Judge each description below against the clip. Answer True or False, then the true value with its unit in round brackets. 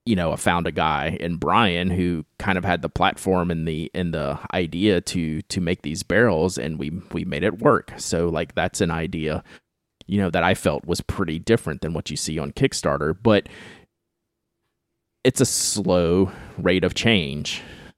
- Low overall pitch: True (85 Hz)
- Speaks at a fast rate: False (185 wpm)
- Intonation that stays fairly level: False (3.3 semitones)